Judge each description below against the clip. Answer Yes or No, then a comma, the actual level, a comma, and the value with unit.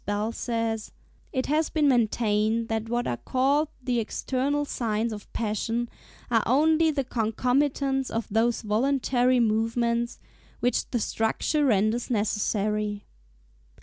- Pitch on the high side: Yes, high, 235 Hz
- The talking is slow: Yes, slow, 120 wpm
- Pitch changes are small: No, average, 3.1 semitones